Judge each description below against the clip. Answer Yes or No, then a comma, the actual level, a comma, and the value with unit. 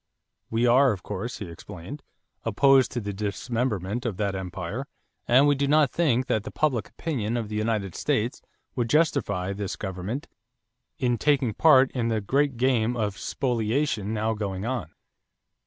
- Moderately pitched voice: No, low, 115 Hz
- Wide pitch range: No, average, 4.4 semitones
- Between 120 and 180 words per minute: Yes, average, 160 wpm